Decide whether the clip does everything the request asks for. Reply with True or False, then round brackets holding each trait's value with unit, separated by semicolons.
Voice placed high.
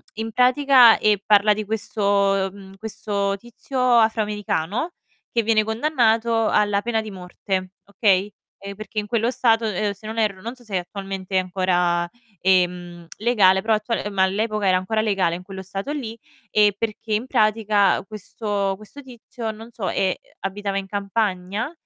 True (210 Hz)